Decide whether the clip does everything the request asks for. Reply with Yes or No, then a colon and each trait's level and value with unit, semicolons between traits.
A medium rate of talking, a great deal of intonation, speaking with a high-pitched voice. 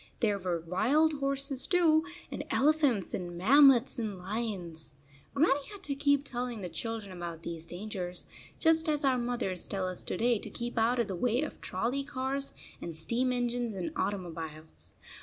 Yes: average, 175 wpm; wide, 7.1 semitones; high, 235 Hz